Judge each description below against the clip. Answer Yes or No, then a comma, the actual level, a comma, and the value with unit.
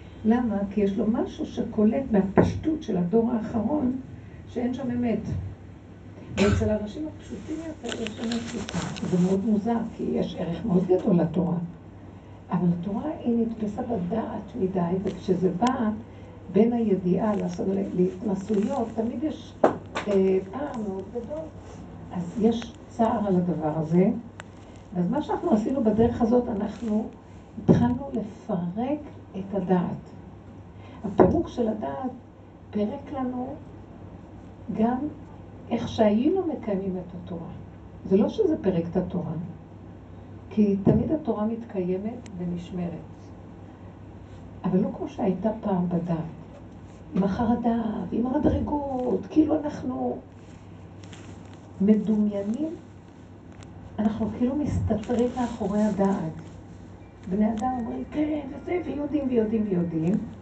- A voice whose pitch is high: Yes, high, 205 Hz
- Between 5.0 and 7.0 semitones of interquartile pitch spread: Yes, wide, 5.4 semitones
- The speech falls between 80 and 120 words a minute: Yes, average, 110 wpm